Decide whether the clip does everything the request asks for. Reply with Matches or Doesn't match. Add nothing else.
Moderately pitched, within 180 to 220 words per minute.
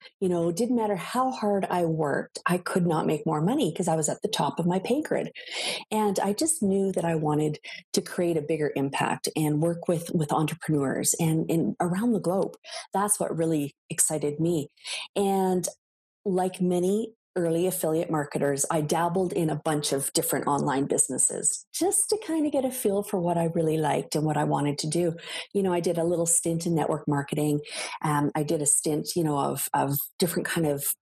Matches